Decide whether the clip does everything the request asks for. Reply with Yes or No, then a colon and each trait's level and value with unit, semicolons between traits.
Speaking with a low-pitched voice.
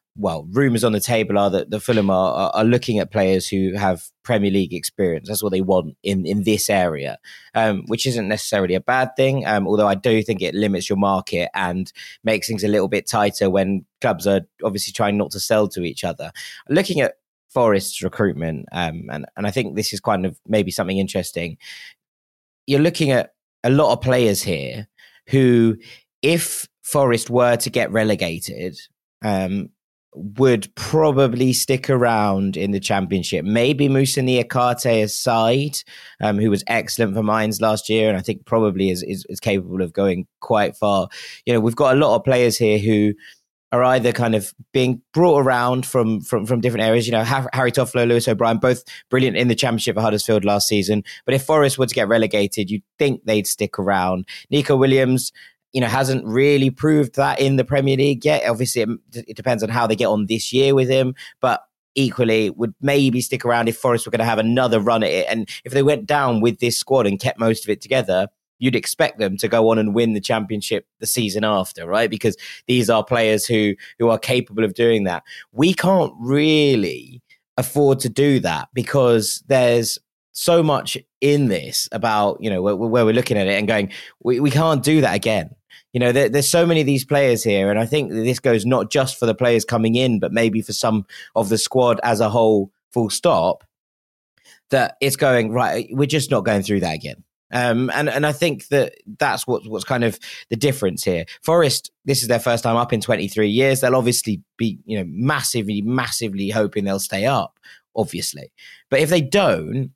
Yes: low, 115 Hz